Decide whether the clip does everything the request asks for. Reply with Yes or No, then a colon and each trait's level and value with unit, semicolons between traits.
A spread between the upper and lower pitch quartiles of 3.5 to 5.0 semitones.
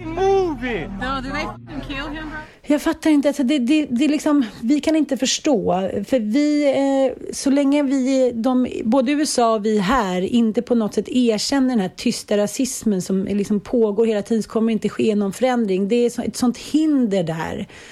Yes: average, 4.6 semitones